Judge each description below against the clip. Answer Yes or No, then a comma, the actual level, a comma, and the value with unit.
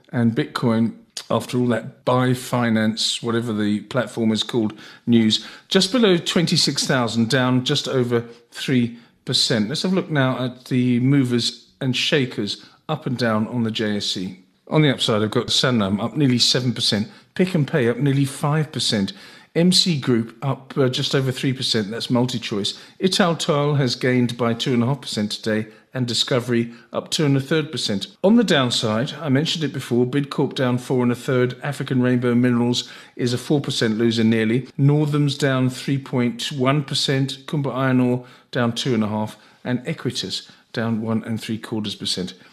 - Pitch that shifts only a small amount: No, average, 3.4 semitones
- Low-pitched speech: Yes, low, 125 Hz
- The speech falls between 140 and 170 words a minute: No, average, 185 wpm